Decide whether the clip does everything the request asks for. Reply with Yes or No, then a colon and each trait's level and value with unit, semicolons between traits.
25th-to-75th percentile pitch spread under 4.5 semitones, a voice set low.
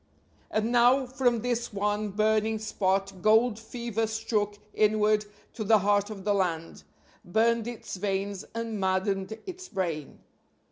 No: narrow, 2.5 semitones; high, 215 Hz